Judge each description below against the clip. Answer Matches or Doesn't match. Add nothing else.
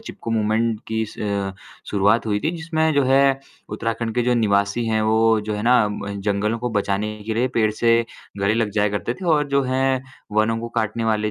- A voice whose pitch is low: Matches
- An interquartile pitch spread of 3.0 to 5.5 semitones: Doesn't match